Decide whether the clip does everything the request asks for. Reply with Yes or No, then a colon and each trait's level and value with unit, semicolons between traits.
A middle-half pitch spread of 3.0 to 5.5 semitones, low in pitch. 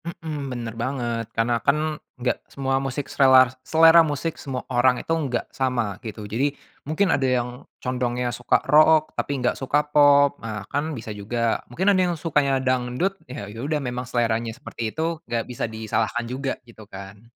Yes: average, 3.6 semitones; low, 130 Hz